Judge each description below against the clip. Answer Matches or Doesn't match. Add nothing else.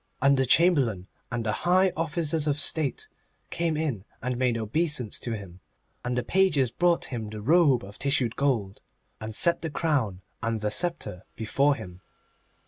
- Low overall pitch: Matches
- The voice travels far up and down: Matches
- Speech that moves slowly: Doesn't match